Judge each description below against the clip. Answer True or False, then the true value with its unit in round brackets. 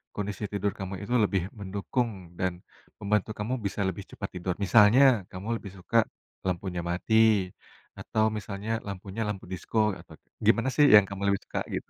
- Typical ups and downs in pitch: False (1.9 semitones)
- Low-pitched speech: True (100 Hz)